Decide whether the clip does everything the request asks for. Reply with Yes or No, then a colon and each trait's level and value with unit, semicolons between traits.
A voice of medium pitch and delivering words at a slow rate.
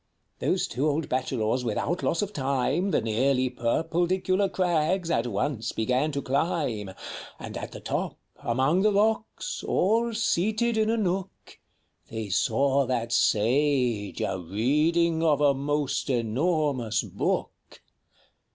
Yes: medium, 145 Hz; slow, 130 wpm